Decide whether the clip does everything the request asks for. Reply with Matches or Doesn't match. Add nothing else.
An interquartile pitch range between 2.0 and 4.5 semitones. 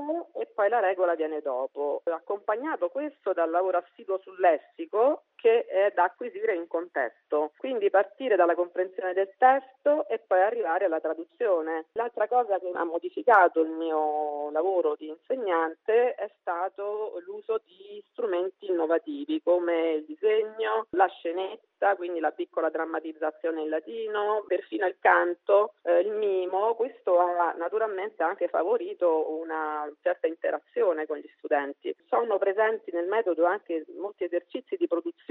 Doesn't match